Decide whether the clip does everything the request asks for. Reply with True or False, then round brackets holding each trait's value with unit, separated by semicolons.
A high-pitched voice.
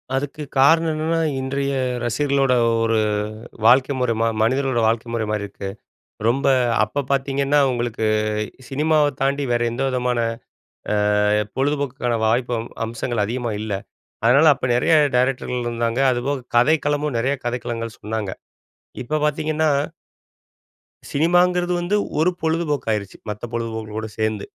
False (130 Hz)